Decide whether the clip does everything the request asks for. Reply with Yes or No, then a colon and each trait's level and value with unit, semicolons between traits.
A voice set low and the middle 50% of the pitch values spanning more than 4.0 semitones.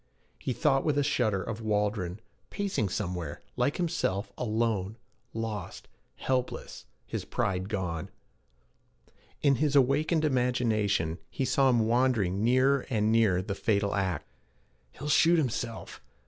Yes: low, 115 Hz; average, 4.9 semitones